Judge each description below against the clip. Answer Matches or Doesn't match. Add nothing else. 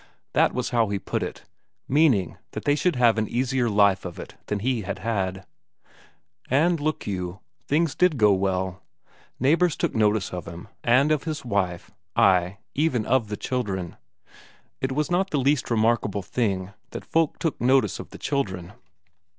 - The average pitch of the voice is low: Matches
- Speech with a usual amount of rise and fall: Doesn't match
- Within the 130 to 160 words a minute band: Doesn't match